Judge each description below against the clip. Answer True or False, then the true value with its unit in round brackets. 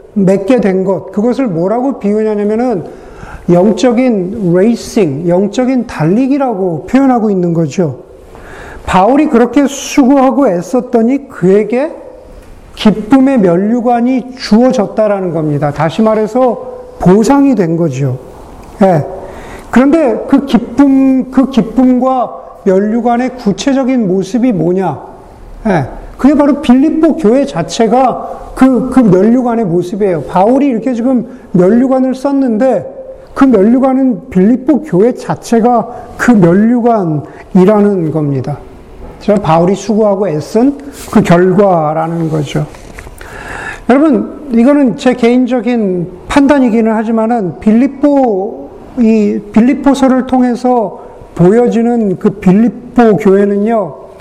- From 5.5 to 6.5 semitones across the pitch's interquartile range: False (5.1 semitones)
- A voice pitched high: True (235 Hz)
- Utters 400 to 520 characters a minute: False (255 characters per minute)